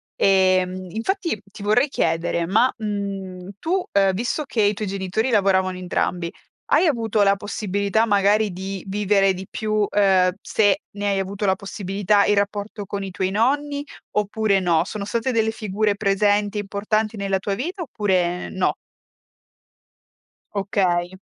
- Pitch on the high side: Yes, high, 200 Hz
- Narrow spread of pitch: Yes, narrow, 2.0 semitones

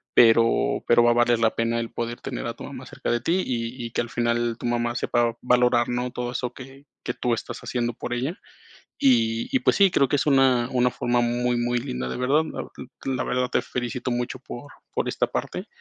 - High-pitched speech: No, low, 120 Hz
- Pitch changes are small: Yes, narrow, 1.3 semitones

